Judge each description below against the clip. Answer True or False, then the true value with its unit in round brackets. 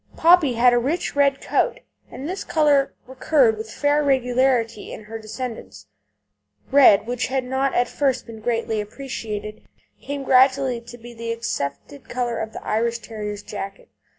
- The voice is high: True (245 Hz)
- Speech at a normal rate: True (155 wpm)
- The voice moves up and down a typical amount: True (3.5 semitones)